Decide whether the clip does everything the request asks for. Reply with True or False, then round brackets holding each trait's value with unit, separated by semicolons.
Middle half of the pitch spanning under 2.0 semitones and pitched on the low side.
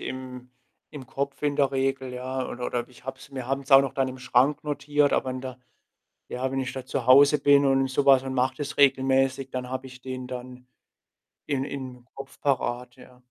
True (1.3 semitones; 130 Hz)